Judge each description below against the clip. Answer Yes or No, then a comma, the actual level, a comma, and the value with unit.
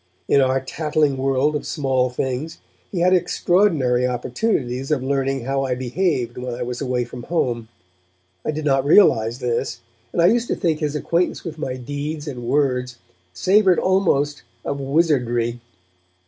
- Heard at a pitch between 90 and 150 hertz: Yes, low, 135 Hz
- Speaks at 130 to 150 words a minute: No, average, 160 wpm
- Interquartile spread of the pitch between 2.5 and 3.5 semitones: No, average, 3.9 semitones